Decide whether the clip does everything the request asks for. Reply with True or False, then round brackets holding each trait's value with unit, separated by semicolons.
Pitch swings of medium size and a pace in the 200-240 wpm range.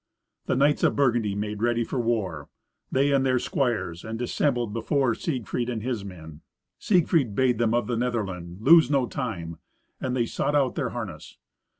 False (4.0 semitones; 175 wpm)